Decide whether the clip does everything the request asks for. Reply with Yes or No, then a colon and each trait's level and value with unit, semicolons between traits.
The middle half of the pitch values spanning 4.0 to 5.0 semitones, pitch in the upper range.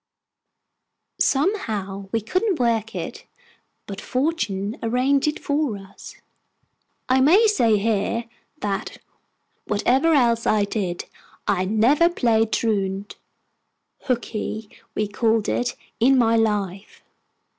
Yes: average, 4.3 semitones; high, 225 Hz